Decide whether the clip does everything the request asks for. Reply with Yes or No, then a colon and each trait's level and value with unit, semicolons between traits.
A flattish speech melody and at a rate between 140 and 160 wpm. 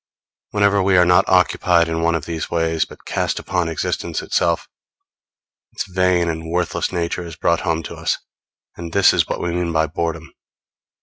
No: narrow, 1.5 semitones; average, 180 wpm